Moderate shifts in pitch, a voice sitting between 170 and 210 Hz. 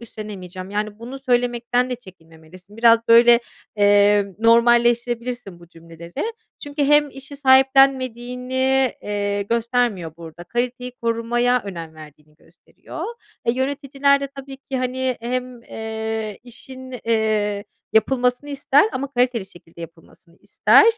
No: average, 4.0 semitones; high, 235 Hz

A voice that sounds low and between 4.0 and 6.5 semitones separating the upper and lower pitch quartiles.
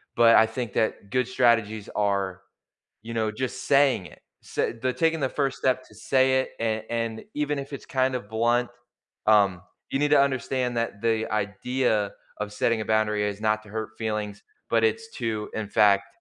No: low, 115 Hz; average, 3.3 semitones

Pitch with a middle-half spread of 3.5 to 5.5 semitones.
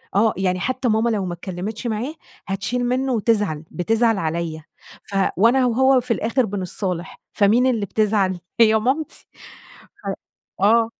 Yes: average, 4.0 semitones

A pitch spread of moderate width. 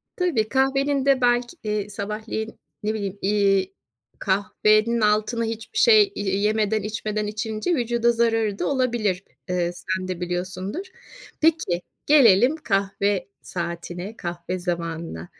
Yes: average, 3.9 semitones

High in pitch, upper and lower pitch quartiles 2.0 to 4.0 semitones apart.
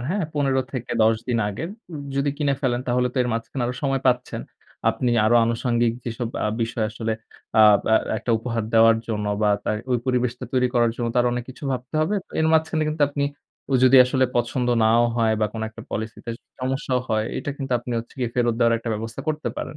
No: low, 120 Hz; narrow, 2.5 semitones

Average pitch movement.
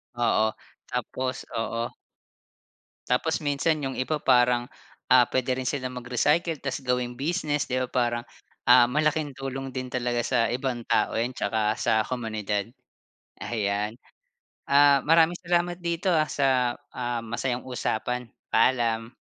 Yes: average, 3.1 semitones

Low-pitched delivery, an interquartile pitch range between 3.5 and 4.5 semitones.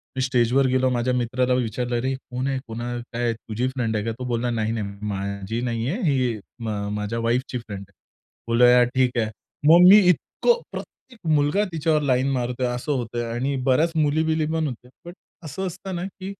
Yes: low, 125 Hz; average, 3.8 semitones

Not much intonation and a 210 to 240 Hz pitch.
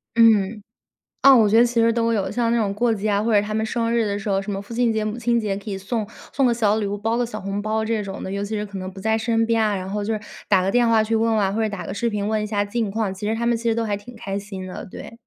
Yes: narrow, 2.2 semitones; high, 215 Hz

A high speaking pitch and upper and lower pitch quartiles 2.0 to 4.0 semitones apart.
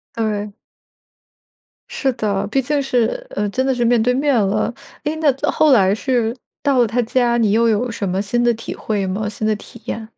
Yes: high, 230 Hz; average, 3.3 semitones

